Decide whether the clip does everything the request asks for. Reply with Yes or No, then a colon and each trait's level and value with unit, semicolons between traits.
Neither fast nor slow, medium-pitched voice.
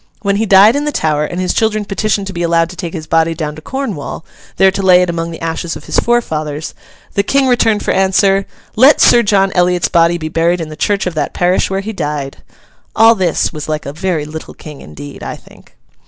No: fast, 230 wpm; medium, 180 Hz